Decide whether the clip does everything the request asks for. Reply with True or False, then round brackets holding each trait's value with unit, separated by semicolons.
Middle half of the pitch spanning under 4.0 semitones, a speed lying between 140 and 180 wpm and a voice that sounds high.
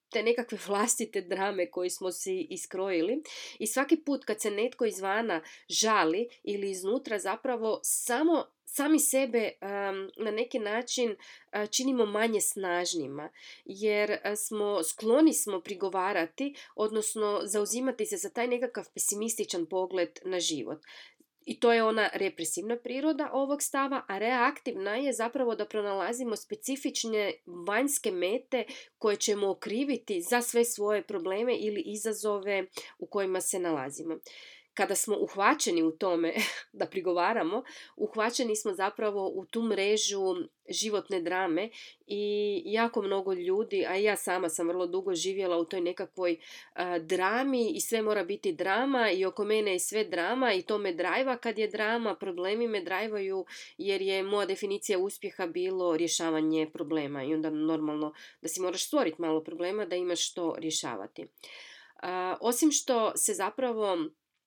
False (4.3 semitones; 145 wpm; 210 Hz)